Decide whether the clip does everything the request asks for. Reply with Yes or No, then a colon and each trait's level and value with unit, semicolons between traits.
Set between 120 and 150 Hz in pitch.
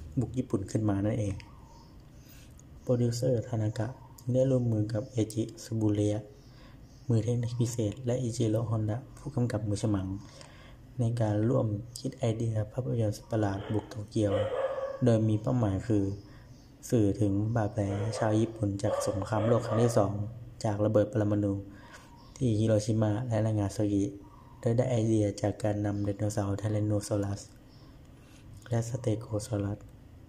No: low, 110 Hz